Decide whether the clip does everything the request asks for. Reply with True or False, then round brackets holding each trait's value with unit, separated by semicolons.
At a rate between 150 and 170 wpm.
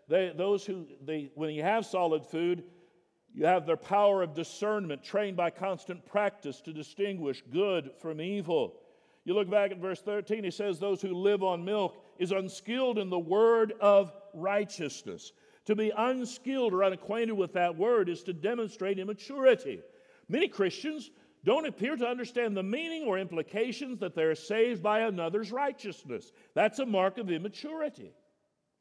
True (160 wpm)